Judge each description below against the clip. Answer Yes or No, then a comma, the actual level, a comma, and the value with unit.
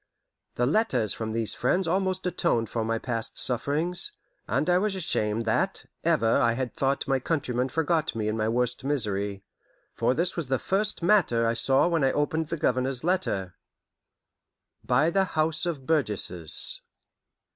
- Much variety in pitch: Yes, wide, 6.6 semitones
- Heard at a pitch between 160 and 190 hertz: No, low, 135 Hz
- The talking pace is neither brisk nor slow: Yes, average, 160 wpm